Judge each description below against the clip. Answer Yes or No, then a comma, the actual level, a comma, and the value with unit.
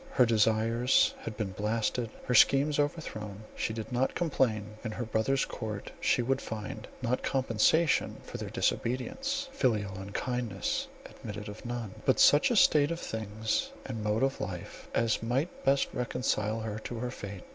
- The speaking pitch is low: Yes, low, 115 Hz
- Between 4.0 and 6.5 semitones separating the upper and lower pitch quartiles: No, average, 3.6 semitones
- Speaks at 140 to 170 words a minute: Yes, average, 160 wpm